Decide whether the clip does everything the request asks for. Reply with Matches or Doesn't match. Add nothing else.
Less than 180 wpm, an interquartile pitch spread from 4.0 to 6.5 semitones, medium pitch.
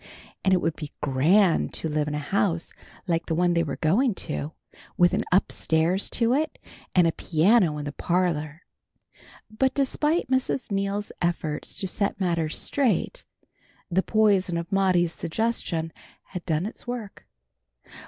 Matches